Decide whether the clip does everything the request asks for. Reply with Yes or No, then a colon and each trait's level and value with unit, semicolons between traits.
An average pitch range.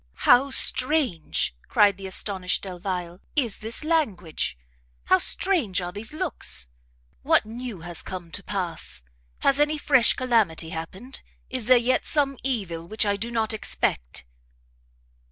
No: wide, 6.3 semitones